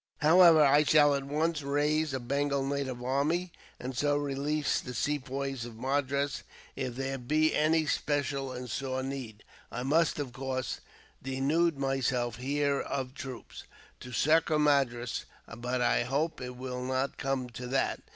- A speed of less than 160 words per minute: Yes, average, 150 wpm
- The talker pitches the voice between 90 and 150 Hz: Yes, low, 135 Hz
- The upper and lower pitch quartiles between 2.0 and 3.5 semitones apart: Yes, narrow, 2.4 semitones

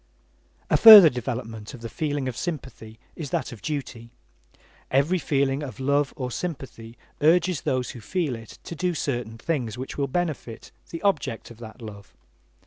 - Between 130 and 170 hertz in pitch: Yes, low, 135 Hz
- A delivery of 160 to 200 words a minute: Yes, average, 165 wpm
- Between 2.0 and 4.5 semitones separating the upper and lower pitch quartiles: No, average, 5.0 semitones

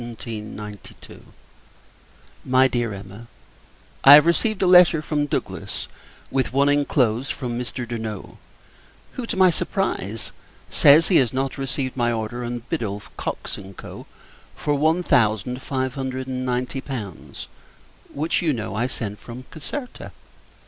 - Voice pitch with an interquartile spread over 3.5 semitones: Yes, average, 4.1 semitones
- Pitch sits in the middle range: No, low, 130 Hz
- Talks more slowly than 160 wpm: Yes, average, 140 wpm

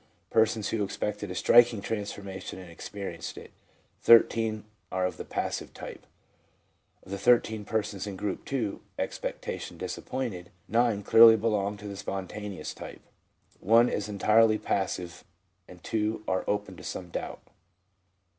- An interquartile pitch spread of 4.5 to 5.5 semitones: No, narrow, 2.5 semitones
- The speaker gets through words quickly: No, average, 140 wpm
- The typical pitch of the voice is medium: No, low, 105 Hz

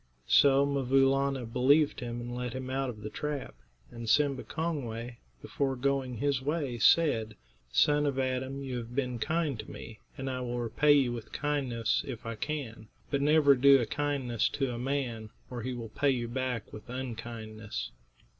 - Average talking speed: Yes, average, 180 wpm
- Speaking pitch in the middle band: No, low, 130 Hz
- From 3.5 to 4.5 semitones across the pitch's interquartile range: No, average, 2.9 semitones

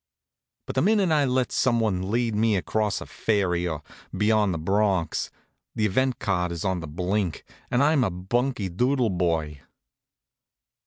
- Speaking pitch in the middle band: No, low, 105 Hz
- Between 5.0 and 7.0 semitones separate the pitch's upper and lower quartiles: Yes, wide, 5.5 semitones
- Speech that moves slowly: No, average, 160 wpm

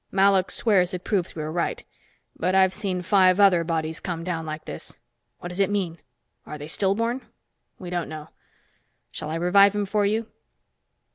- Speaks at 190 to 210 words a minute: No, average, 180 wpm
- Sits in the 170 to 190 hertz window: Yes, medium, 185 Hz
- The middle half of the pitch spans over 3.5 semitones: No, average, 3.1 semitones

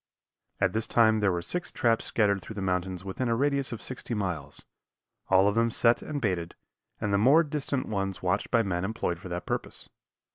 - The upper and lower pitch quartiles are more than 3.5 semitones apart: Yes, average, 4.1 semitones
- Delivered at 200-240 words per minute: Yes, fast, 205 wpm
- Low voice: Yes, low, 105 Hz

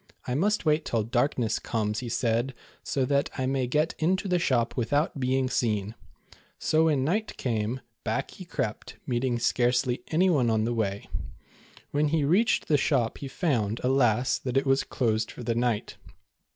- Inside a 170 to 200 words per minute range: Yes, average, 175 wpm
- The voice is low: Yes, low, 130 Hz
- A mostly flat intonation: No, average, 3.9 semitones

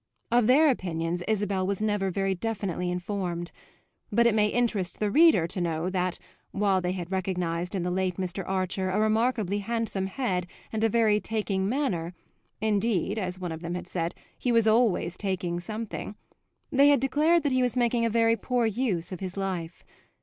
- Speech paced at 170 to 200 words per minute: Yes, average, 185 wpm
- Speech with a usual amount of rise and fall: Yes, average, 4.1 semitones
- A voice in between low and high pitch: No, high, 195 Hz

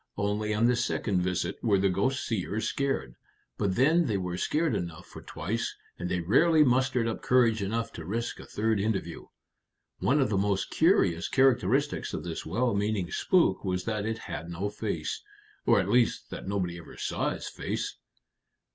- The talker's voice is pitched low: Yes, low, 105 Hz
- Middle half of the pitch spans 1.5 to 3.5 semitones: No, average, 5.1 semitones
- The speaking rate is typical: Yes, average, 180 wpm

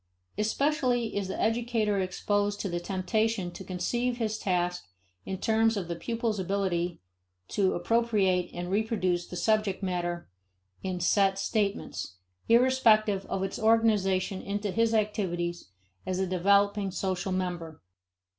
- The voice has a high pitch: Yes, high, 195 Hz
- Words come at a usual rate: No, slow, 130 wpm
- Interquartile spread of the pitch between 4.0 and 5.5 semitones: No, average, 3.2 semitones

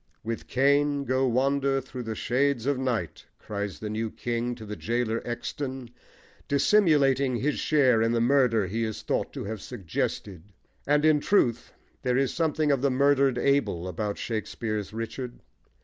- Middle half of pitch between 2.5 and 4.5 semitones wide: Yes, average, 3.8 semitones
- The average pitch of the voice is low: Yes, low, 125 Hz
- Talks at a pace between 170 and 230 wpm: No, average, 160 wpm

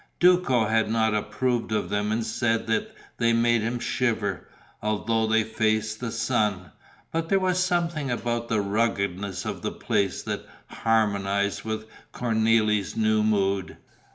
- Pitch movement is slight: Yes, narrow, 2.0 semitones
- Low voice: Yes, low, 110 Hz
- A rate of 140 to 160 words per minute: Yes, average, 145 wpm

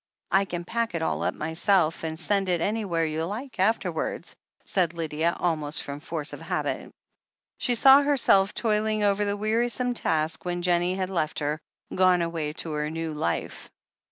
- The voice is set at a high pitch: No, medium, 175 Hz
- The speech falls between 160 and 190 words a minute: Yes, average, 170 wpm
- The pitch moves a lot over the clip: No, average, 4.4 semitones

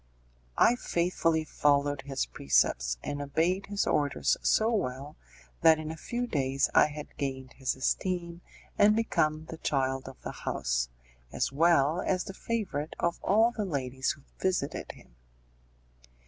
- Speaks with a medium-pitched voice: Yes, medium, 150 Hz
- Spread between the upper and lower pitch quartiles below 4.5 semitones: No, average, 5.2 semitones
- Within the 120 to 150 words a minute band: Yes, average, 145 wpm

